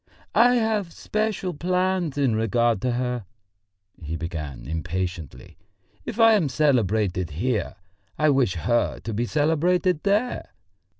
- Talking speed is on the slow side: Yes, slow, 125 wpm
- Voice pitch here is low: Yes, low, 125 Hz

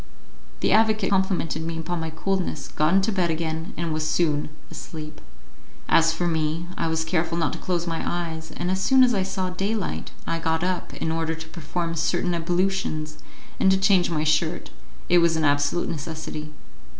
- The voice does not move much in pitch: Yes, narrow, 2.3 semitones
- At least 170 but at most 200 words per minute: Yes, average, 185 wpm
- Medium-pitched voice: Yes, medium, 165 Hz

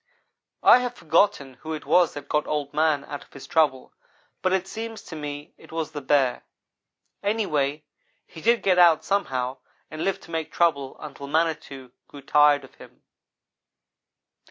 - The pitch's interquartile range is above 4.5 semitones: No, average, 3.7 semitones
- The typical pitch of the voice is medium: Yes, medium, 155 Hz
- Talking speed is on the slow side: No, average, 170 wpm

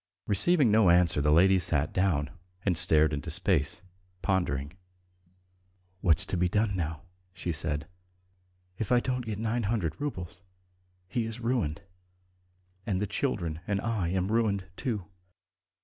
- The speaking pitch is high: No, very low, 95 Hz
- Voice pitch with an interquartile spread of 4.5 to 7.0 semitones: Yes, average, 5.1 semitones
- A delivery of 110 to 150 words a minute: Yes, average, 140 wpm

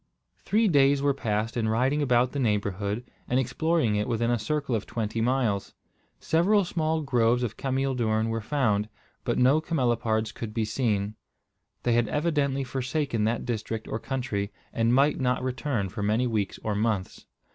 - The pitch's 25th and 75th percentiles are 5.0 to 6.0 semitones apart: No, average, 3.8 semitones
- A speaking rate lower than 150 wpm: No, average, 170 wpm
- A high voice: No, low, 120 Hz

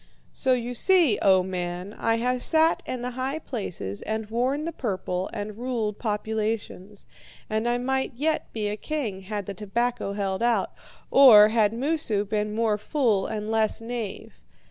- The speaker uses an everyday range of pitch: Yes, average, 3.3 semitones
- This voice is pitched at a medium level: No, high, 220 Hz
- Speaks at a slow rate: No, average, 165 wpm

